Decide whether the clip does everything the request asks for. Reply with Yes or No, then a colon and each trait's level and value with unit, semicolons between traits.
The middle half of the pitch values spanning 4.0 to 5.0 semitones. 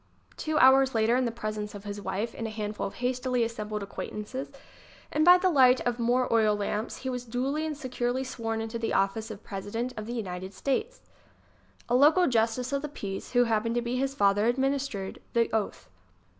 No: average, 3.5 semitones